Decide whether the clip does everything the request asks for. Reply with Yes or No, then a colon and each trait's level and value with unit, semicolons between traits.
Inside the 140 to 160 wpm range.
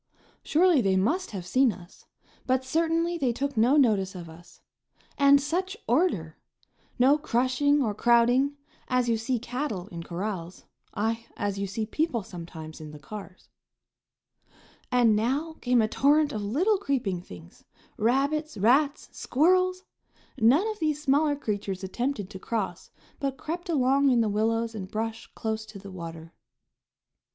Yes: average, 150 wpm